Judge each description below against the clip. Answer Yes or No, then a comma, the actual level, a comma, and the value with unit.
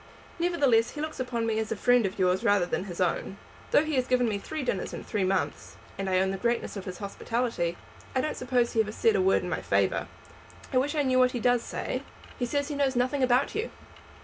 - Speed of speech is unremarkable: No, fast, 245 wpm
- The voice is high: Yes, high, 245 Hz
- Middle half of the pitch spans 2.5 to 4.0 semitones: No, average, 4.8 semitones